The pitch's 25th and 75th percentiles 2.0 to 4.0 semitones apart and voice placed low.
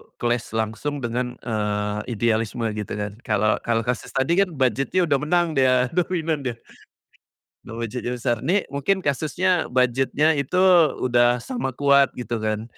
No: average, 4.5 semitones; low, 125 Hz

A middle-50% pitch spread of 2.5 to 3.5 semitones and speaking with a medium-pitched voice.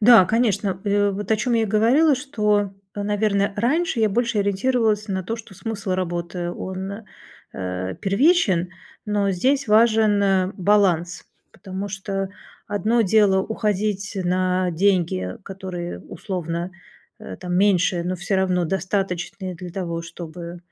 No: average, 2.9 semitones; high, 195 Hz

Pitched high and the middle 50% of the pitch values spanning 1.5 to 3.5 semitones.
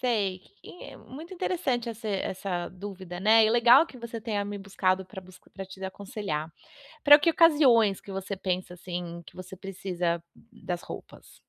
No: high, 195 Hz; average, 4.1 semitones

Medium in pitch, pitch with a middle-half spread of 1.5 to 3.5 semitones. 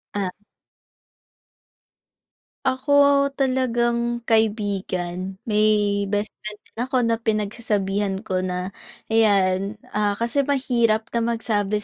No: high, 215 Hz; average, 2.9 semitones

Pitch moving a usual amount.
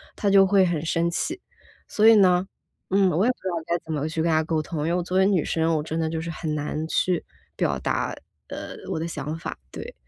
Yes: average, 3.0 semitones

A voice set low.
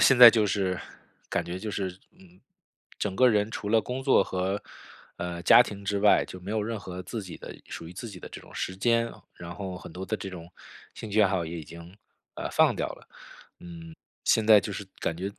Yes: low, 100 Hz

